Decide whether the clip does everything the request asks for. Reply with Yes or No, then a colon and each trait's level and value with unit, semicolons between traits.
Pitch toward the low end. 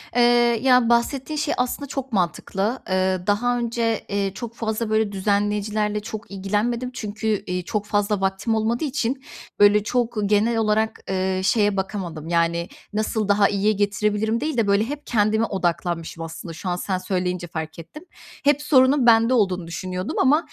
No: high, 210 Hz